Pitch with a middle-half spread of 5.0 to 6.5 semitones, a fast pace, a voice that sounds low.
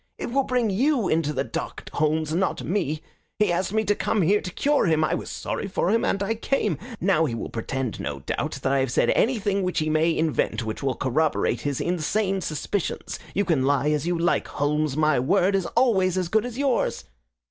No: average, 5.3 semitones; fast, 215 wpm; medium, 175 Hz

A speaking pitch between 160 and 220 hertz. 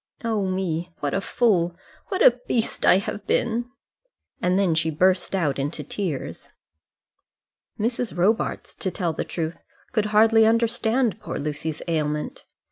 Yes: high, 190 Hz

